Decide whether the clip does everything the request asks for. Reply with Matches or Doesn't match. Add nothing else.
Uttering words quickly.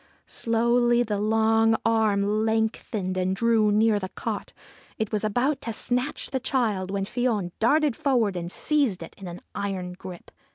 Doesn't match